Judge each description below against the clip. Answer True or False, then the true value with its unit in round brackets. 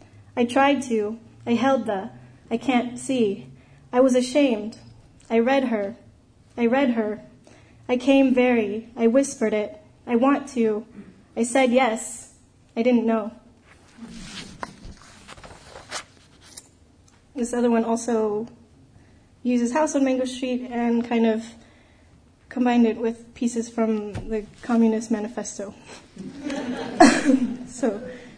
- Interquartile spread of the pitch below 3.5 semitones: True (2.6 semitones)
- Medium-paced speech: False (115 wpm)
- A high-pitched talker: True (235 Hz)